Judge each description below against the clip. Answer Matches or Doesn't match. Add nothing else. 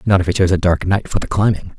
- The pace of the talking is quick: Matches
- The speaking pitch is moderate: Doesn't match